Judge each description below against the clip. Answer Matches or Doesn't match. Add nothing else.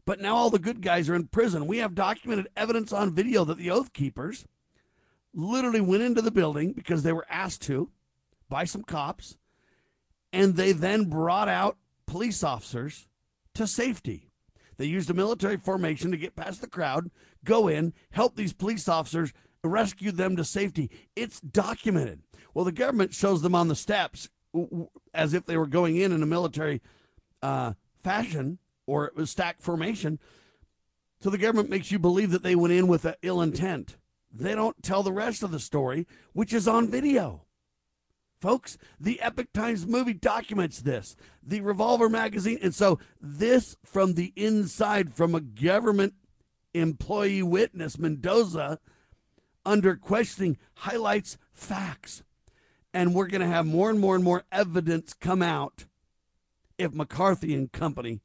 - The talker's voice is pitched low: Doesn't match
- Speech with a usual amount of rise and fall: Matches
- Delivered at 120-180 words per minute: Matches